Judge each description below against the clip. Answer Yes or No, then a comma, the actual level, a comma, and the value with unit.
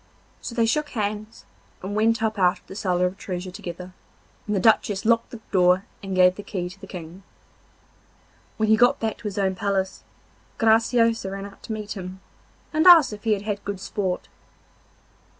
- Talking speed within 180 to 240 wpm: Yes, average, 190 wpm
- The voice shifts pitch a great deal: No, average, 2.9 semitones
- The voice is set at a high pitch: Yes, high, 205 Hz